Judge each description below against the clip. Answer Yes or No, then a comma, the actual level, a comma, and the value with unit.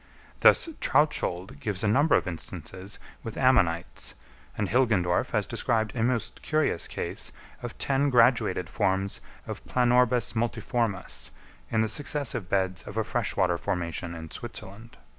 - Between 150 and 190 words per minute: No, average, 140 wpm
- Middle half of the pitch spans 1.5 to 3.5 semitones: No, average, 4.8 semitones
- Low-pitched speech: Yes, low, 110 Hz